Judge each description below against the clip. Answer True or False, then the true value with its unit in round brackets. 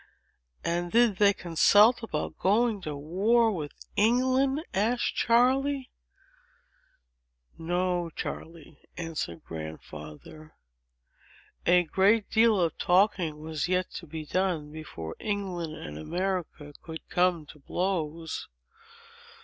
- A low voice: False (180 Hz)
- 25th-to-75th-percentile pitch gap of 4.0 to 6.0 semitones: True (5.1 semitones)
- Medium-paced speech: False (105 wpm)